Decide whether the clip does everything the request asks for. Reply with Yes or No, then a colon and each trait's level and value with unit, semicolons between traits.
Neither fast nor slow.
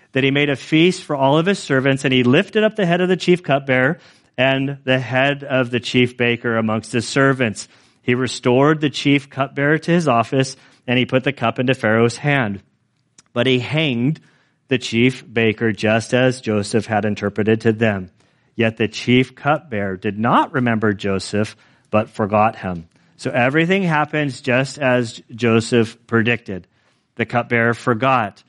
Yes: average, 170 wpm